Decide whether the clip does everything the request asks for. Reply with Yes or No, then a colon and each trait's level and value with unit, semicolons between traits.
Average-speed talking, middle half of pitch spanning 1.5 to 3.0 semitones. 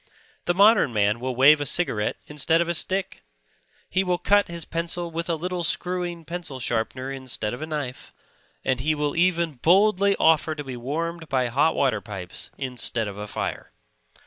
No: average, 180 wpm; average, 5.2 semitones